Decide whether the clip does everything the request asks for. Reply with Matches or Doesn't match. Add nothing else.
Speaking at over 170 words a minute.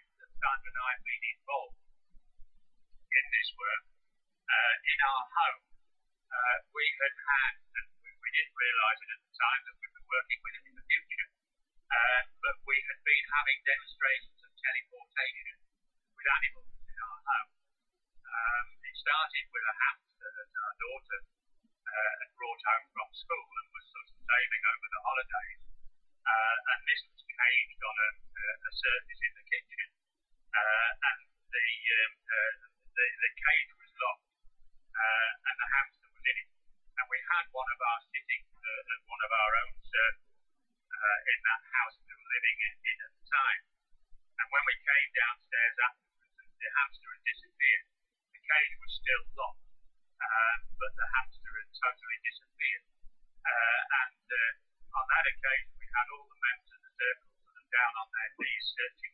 Doesn't match